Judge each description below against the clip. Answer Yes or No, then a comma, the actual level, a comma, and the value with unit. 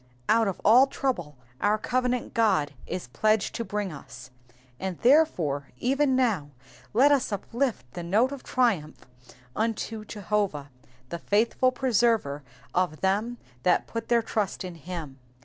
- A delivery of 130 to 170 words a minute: Yes, average, 140 wpm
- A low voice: No, high, 210 Hz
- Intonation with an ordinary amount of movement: No, wide, 6.0 semitones